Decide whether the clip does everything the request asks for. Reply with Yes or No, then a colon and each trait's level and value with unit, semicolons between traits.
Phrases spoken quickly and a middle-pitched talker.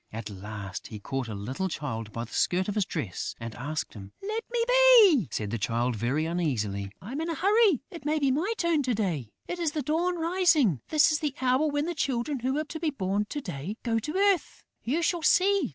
No: fast, 230 wpm; high, 245 Hz